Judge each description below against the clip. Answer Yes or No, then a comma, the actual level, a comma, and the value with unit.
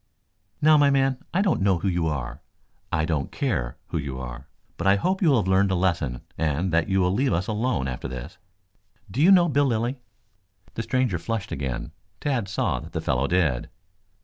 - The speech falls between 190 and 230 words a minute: Yes, average, 200 wpm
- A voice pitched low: Yes, very low, 95 Hz